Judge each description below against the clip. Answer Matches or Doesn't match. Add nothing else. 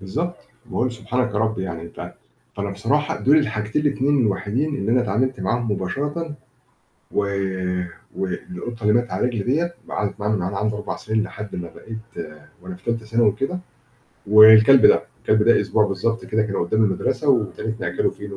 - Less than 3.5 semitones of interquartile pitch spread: Doesn't match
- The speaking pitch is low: Matches